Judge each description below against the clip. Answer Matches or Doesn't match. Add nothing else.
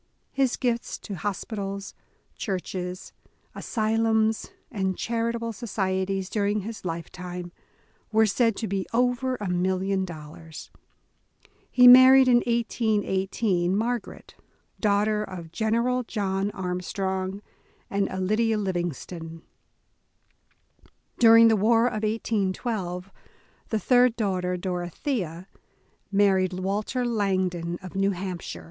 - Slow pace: Matches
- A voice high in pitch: Matches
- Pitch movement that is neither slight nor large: Matches